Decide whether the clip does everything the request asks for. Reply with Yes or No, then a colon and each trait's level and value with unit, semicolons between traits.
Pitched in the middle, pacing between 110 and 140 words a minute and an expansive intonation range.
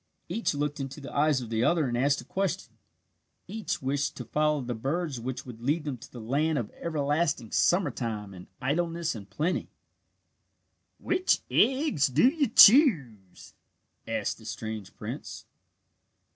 No: medium, 145 Hz; average, 155 wpm; wide, 5.8 semitones